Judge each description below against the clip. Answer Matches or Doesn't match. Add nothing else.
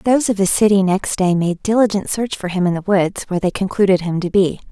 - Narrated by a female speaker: Matches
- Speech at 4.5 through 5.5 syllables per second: Doesn't match